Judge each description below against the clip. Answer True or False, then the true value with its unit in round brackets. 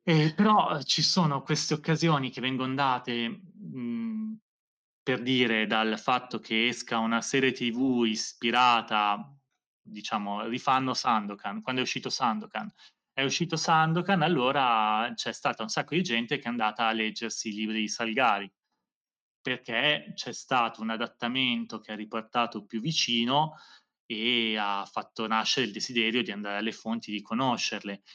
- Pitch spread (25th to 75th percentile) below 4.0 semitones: False (5.1 semitones)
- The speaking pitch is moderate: False (120 Hz)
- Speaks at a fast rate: False (145 wpm)